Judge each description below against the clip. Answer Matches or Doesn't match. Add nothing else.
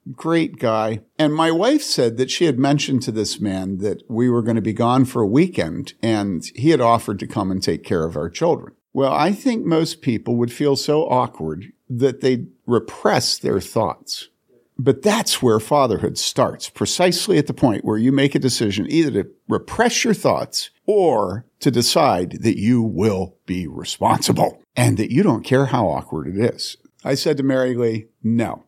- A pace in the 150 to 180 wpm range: Doesn't match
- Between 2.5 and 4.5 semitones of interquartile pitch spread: Doesn't match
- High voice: Doesn't match